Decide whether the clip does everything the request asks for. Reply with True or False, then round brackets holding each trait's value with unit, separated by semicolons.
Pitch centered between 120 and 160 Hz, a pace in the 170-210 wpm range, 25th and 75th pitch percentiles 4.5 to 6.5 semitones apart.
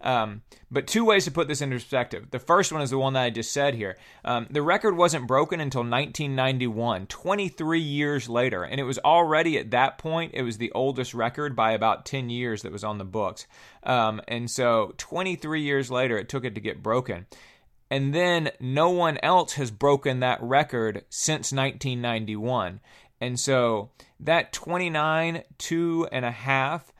True (135 Hz; 180 wpm; 4.8 semitones)